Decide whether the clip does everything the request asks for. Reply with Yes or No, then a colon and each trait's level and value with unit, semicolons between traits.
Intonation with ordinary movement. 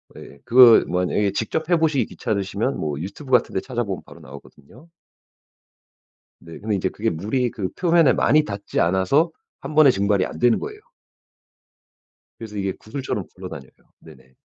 No: wide, 6.0 semitones